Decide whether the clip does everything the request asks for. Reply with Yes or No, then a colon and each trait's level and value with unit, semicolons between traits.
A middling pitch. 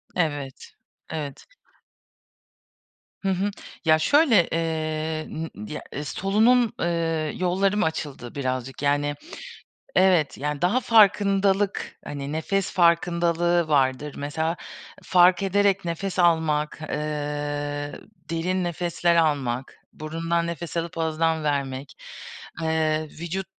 Yes: medium, 165 Hz